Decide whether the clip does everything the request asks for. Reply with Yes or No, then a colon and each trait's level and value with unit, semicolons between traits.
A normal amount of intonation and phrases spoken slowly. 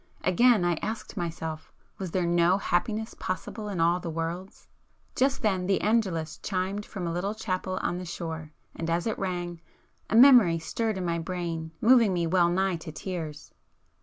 No: average, 3.3 semitones; average, 170 wpm